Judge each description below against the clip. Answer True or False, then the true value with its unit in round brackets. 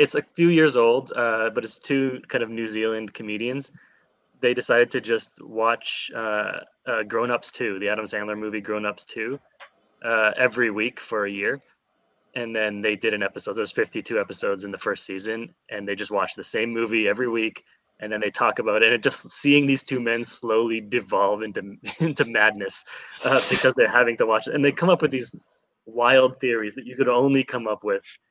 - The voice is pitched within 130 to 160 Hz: False (115 Hz)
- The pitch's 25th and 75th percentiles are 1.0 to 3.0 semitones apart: False (3.8 semitones)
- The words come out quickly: True (210 wpm)